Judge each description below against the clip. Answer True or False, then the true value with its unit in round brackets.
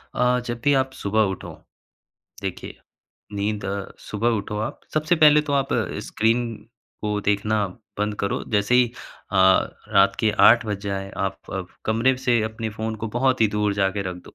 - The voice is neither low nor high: False (110 Hz)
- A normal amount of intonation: True (3.2 semitones)